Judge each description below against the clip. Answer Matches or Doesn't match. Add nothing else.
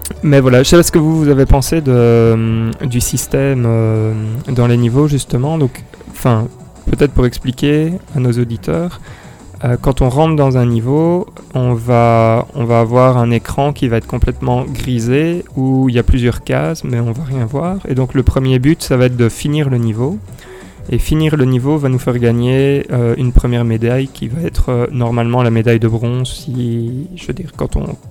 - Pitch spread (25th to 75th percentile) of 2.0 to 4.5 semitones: Matches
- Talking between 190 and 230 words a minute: Matches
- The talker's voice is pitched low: Matches